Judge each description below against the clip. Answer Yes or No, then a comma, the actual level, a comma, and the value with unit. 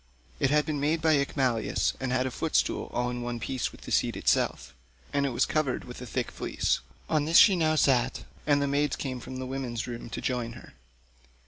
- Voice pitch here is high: No, low, 130 Hz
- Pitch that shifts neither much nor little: Yes, average, 3.1 semitones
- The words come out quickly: Yes, fast, 220 wpm